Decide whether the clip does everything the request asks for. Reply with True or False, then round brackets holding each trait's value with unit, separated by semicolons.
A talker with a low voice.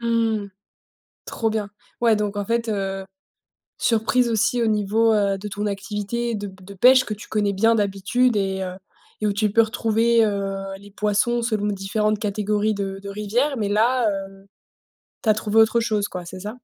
False (210 Hz)